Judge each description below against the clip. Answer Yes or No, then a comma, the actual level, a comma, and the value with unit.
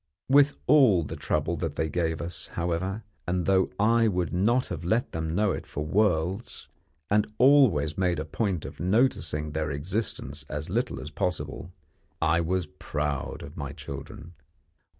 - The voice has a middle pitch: No, very low, 90 Hz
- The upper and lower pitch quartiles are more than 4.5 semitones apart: Yes, average, 5.2 semitones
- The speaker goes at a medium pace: Yes, average, 160 wpm